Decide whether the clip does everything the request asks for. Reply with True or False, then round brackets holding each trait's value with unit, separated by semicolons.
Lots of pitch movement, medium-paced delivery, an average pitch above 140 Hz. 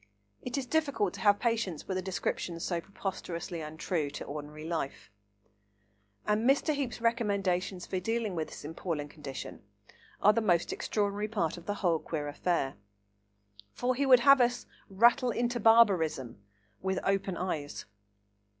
True (5.9 semitones; 150 wpm; 190 Hz)